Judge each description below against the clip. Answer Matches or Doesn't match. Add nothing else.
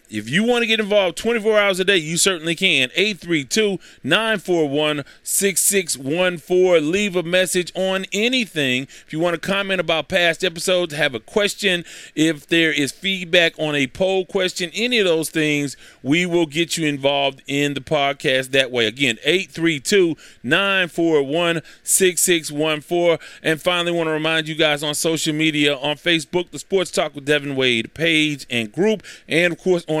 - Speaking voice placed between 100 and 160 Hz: Doesn't match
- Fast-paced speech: Doesn't match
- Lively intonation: Doesn't match